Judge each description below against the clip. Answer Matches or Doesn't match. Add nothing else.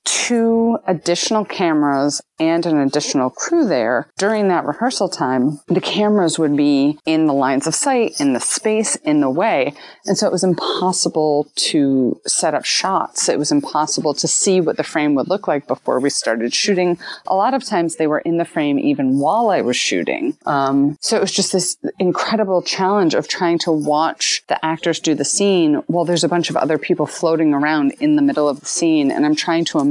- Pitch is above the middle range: Doesn't match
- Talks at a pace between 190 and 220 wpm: Matches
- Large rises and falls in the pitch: Matches